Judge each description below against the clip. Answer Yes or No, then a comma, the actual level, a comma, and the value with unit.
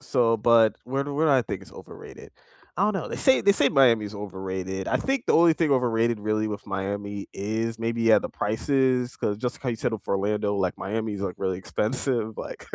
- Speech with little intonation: No, average, 3.8 semitones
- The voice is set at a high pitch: No, low, 115 Hz